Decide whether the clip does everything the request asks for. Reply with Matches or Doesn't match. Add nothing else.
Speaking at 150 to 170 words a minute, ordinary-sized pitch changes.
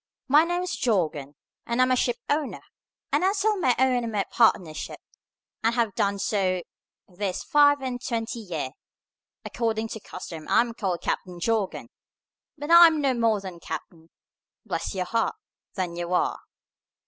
Doesn't match